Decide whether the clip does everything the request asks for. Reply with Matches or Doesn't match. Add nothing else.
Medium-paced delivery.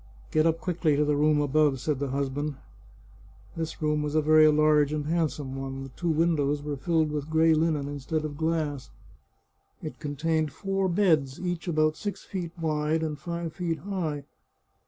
Matches